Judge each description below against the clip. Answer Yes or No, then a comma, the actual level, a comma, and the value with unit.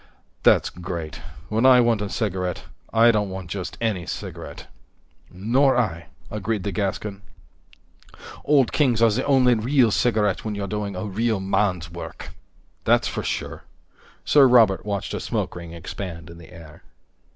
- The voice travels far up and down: No, average, 4.1 semitones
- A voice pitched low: Yes, low, 105 Hz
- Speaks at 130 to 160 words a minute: Yes, average, 155 wpm